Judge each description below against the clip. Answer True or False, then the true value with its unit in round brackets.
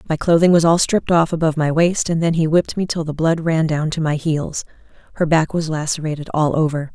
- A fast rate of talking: True (240 wpm)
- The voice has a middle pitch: True (160 Hz)